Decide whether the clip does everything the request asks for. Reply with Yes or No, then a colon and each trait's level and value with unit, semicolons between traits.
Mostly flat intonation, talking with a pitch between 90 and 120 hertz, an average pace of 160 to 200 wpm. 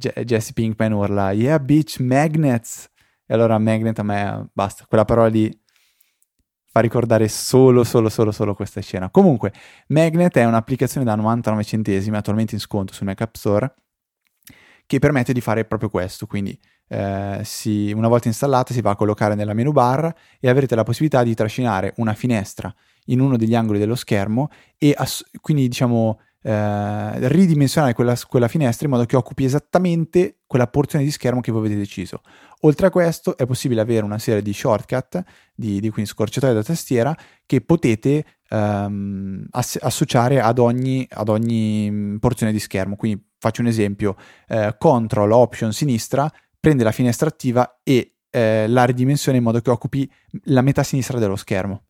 No: average, 3.7 semitones; low, 115 Hz; fast, 170 wpm